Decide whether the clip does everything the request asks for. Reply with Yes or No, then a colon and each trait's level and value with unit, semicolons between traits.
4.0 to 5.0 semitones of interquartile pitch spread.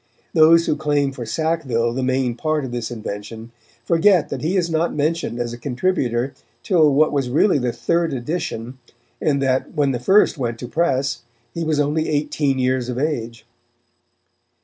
Yes: average, 4.5 semitones